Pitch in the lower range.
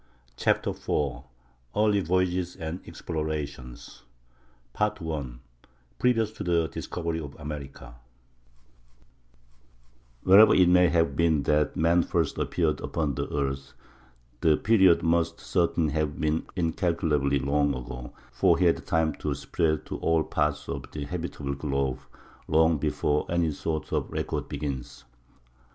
Yes: very low, 80 Hz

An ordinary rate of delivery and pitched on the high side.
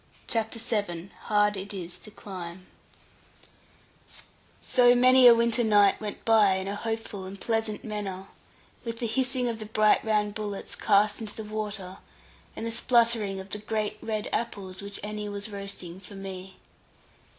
Yes: average, 160 wpm; high, 210 Hz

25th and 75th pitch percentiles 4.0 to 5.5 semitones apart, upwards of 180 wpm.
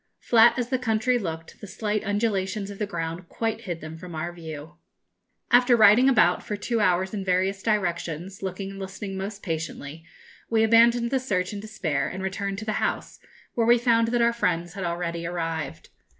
Yes: average, 4.4 semitones; average, 190 wpm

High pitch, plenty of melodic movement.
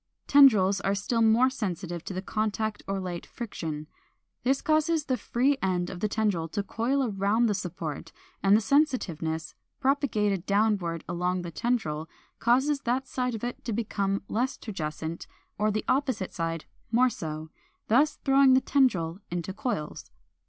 Yes: high, 210 Hz; wide, 6.1 semitones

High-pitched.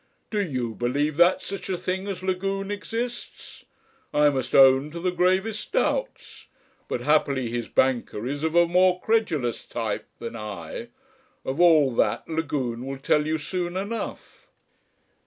No: medium, 160 Hz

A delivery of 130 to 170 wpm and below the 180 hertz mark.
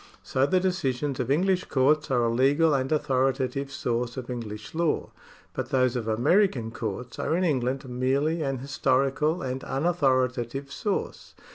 Yes: average, 155 wpm; low, 135 Hz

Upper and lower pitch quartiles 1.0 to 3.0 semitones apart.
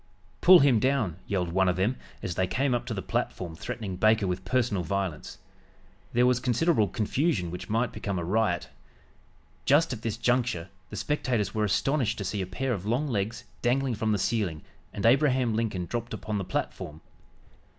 No: average, 5.0 semitones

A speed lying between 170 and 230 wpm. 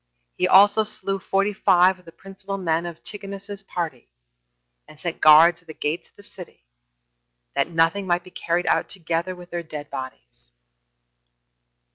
No: average, 160 wpm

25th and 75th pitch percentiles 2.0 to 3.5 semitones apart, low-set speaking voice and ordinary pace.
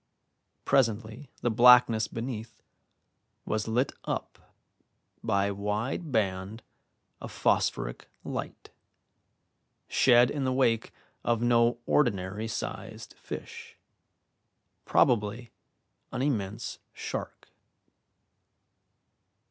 No: average, 2.9 semitones; low, 115 Hz; slow, 85 wpm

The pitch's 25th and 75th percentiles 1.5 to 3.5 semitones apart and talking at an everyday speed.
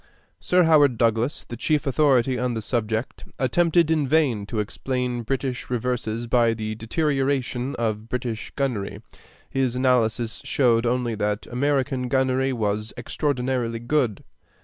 No: average, 2.8 semitones; slow, 130 wpm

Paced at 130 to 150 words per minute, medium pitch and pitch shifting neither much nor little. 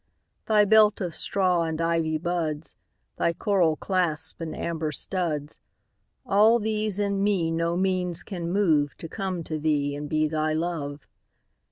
Yes: slow, 135 wpm; medium, 170 Hz; average, 3.8 semitones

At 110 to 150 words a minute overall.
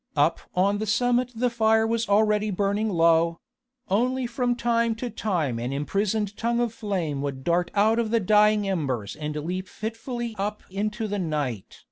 No: average, 170 wpm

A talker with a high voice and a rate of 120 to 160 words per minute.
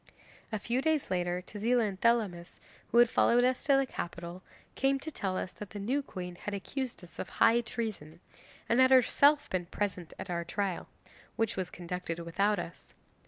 No: high, 205 Hz; average, 185 wpm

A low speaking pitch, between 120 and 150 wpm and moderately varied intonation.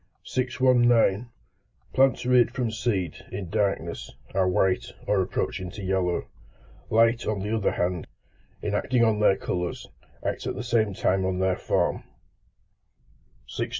Yes: low, 105 Hz; average, 140 wpm; average, 4.2 semitones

